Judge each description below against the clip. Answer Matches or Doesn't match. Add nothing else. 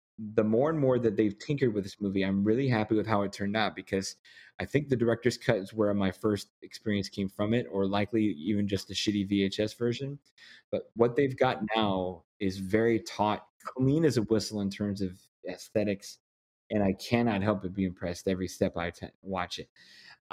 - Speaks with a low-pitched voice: Matches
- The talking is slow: Doesn't match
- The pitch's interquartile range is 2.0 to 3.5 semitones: Matches